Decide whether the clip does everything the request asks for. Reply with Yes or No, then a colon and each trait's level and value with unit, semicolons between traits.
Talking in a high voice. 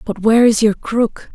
Yes: high, 215 Hz